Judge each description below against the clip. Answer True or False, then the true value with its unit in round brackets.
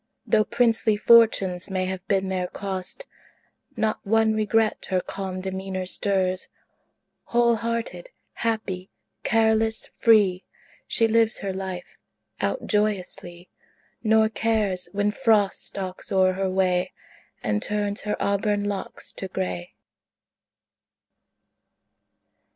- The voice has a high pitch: True (200 Hz)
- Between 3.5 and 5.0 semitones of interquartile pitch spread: False (2.9 semitones)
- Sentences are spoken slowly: True (110 wpm)